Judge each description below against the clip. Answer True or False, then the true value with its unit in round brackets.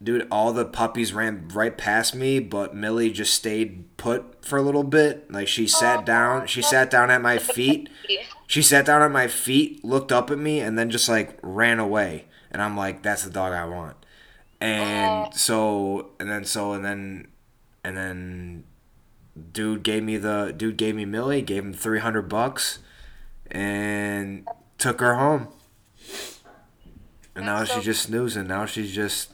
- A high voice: False (110 Hz)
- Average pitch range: True (3.4 semitones)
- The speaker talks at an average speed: True (170 wpm)